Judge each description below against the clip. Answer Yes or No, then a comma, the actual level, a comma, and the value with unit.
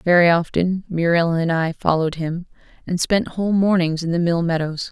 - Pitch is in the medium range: Yes, medium, 170 Hz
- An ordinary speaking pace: Yes, average, 185 wpm